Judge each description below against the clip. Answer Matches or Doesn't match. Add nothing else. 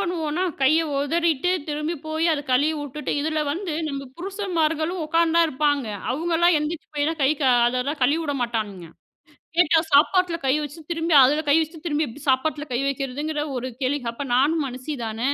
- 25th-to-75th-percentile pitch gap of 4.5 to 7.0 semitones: Doesn't match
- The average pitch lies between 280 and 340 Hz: Matches